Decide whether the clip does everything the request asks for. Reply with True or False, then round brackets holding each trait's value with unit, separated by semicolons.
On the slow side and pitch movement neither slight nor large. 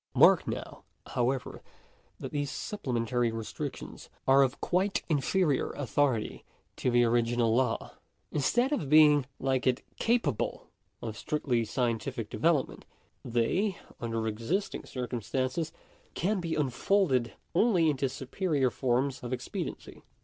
True (115 wpm; 4.5 semitones)